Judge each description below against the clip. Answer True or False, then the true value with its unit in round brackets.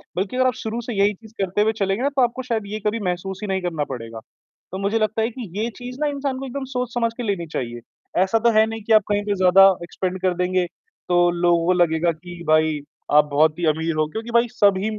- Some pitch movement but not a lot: True (4.6 semitones)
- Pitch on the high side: True (195 Hz)